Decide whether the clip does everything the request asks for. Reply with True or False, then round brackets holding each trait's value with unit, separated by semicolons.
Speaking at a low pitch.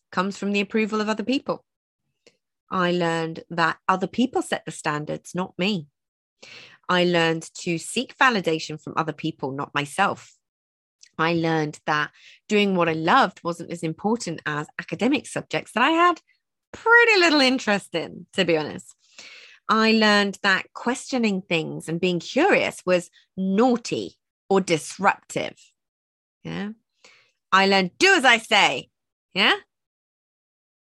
False (185 Hz)